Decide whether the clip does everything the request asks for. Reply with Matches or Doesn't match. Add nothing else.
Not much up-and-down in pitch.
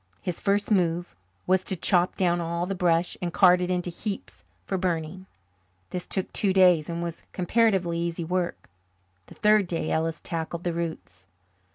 Matches